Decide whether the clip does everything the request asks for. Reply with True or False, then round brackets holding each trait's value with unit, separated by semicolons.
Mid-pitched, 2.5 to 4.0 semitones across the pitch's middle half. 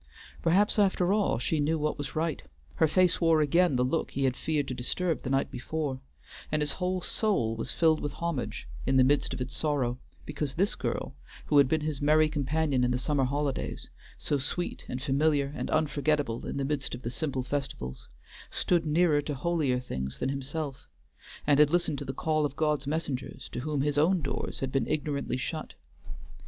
True (145 Hz; 2.9 semitones)